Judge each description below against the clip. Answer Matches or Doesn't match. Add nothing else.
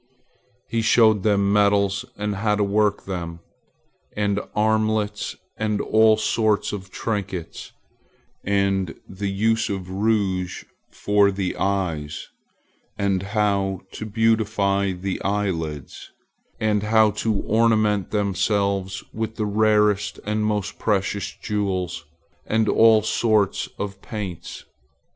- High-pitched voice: Doesn't match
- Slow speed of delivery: Matches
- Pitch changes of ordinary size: Doesn't match